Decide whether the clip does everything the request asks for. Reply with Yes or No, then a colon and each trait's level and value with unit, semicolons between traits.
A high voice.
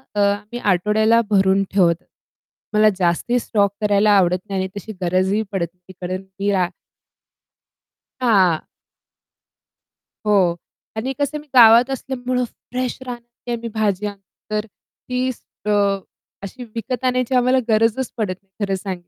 Yes: high, 210 Hz